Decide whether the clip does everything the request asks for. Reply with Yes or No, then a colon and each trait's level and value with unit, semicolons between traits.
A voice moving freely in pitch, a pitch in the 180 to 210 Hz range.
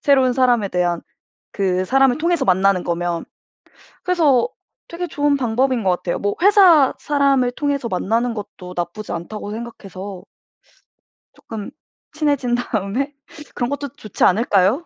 No: wide, 6.4 semitones; high, 240 Hz